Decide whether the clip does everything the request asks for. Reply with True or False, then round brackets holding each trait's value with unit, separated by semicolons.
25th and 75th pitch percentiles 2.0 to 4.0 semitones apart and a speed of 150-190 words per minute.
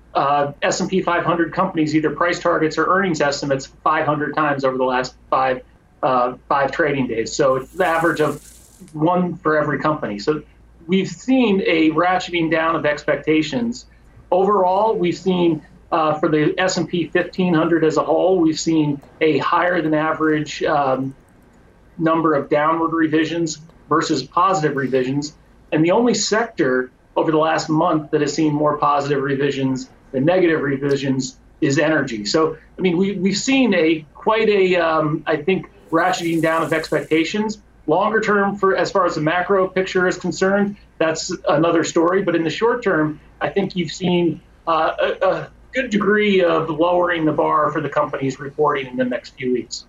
True (3.2 semitones; 165 wpm)